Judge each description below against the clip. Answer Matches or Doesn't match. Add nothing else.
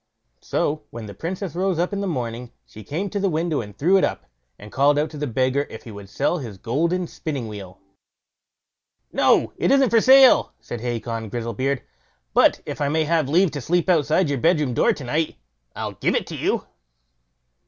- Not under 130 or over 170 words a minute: Doesn't match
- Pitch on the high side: Doesn't match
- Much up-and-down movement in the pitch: Matches